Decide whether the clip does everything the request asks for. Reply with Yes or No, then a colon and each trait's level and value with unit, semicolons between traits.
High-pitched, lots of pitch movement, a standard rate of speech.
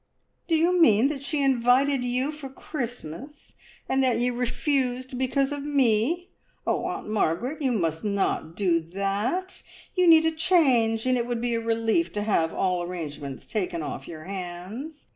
Yes: high, 245 Hz; wide, 6.2 semitones; average, 165 wpm